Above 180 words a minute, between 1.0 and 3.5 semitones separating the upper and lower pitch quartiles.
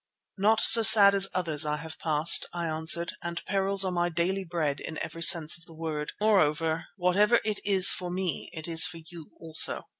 Yes: average, 200 wpm; average, 3.1 semitones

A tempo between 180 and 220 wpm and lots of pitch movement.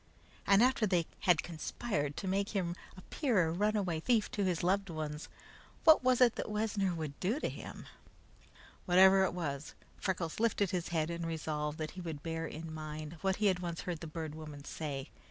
No: average, 190 wpm; average, 4.0 semitones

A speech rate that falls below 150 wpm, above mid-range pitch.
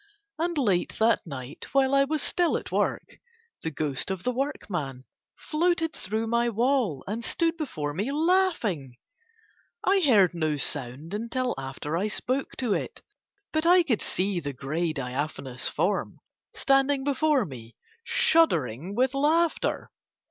Yes: average, 140 wpm; high, 225 Hz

